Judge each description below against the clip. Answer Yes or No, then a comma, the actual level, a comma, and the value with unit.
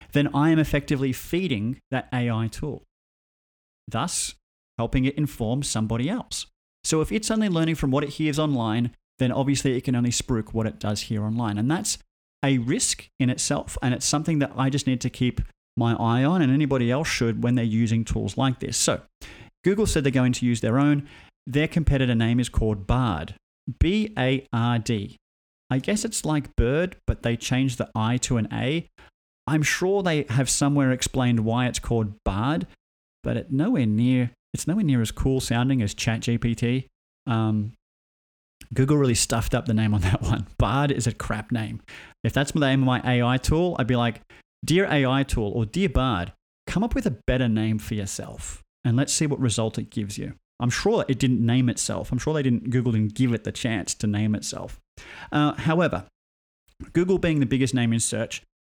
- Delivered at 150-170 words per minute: No, average, 200 wpm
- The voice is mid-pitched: No, low, 125 Hz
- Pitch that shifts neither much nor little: Yes, average, 3.9 semitones